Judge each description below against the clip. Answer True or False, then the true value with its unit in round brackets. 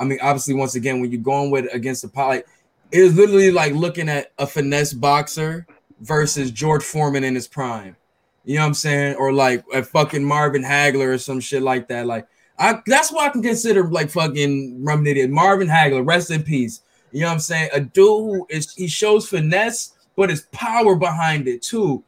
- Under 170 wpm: False (205 wpm)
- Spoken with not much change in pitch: False (4.5 semitones)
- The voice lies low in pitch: False (150 Hz)